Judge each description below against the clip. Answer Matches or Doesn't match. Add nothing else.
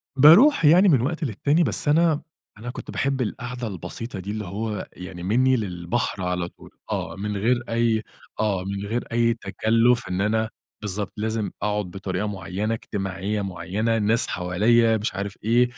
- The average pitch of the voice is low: Matches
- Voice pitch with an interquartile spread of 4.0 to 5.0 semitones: Doesn't match